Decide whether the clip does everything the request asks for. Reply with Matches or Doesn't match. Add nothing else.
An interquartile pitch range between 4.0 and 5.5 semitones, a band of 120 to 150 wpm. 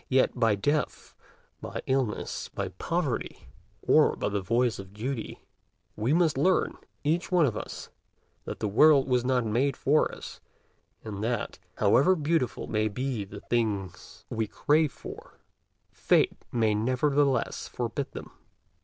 Matches